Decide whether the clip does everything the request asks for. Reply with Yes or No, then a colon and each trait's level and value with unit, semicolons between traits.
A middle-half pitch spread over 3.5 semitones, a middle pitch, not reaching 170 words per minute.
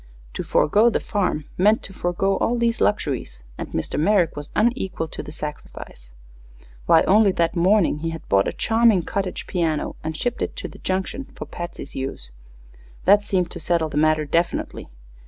No: average, 4.8 semitones; medium, 175 Hz; average, 180 wpm